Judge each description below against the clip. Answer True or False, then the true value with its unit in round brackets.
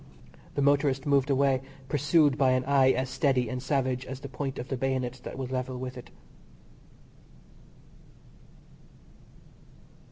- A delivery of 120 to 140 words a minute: True (135 wpm)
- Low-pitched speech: True (130 Hz)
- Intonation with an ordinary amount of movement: False (1.5 semitones)